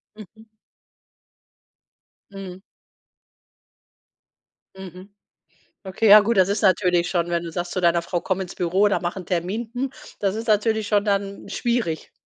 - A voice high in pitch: Yes, high, 195 Hz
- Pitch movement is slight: No, average, 3.0 semitones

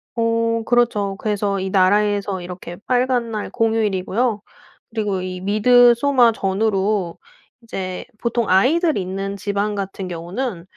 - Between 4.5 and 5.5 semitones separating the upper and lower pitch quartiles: No, average, 3.2 semitones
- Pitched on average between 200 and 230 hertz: Yes, high, 205 Hz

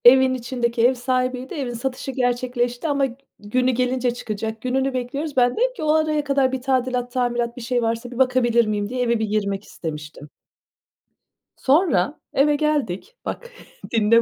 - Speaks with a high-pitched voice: Yes, very high, 250 Hz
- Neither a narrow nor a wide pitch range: No, narrow, 2.2 semitones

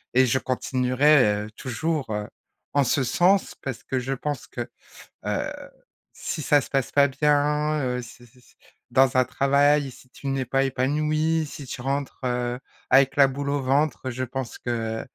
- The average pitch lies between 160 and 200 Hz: No, low, 135 Hz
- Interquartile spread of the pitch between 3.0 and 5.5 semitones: No, narrow, 2.5 semitones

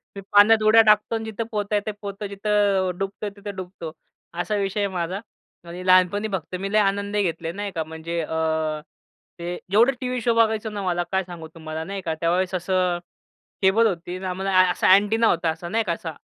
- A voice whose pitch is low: No, high, 190 Hz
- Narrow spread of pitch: No, average, 3.2 semitones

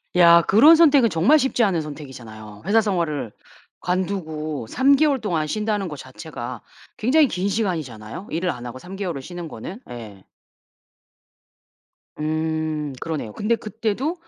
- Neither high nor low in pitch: Yes, medium, 170 Hz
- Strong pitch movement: Yes, wide, 6.4 semitones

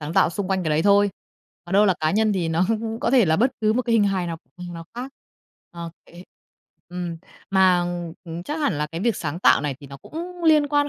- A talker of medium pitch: Yes, medium, 180 Hz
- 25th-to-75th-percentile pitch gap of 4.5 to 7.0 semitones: Yes, average, 4.8 semitones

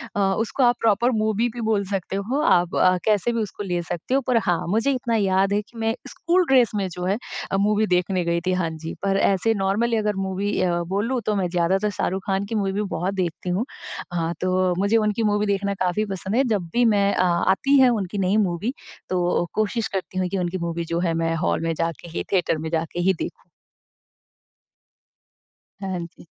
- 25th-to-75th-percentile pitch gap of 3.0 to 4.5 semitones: Yes, average, 3.3 semitones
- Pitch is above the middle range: Yes, high, 195 Hz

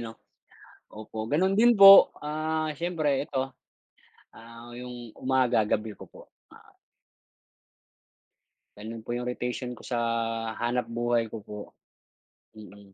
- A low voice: Yes, low, 120 Hz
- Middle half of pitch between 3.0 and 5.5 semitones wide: Yes, average, 4.5 semitones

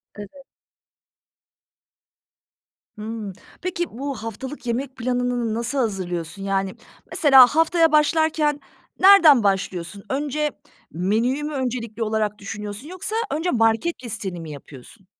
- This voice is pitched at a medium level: No, high, 235 Hz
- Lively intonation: Yes, wide, 6.3 semitones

